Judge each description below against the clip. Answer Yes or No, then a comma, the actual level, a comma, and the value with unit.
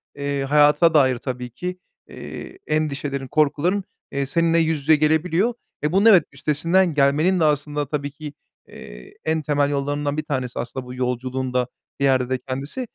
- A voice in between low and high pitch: Yes, medium, 145 Hz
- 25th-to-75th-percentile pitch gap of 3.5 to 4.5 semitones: No, average, 3.0 semitones